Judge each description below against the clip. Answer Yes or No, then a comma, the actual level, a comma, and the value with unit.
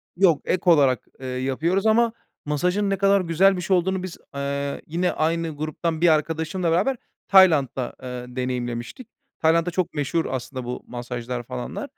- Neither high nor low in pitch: Yes, medium, 160 Hz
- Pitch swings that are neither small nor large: No, wide, 5.8 semitones